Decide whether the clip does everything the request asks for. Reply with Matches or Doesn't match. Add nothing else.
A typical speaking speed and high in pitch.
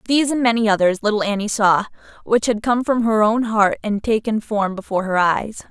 Doesn't match